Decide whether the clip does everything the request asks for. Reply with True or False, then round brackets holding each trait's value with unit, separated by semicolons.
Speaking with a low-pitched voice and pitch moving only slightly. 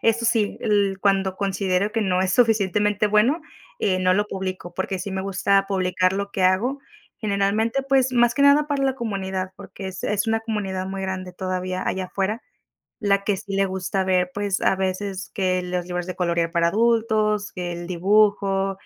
False (195 Hz; 2.2 semitones)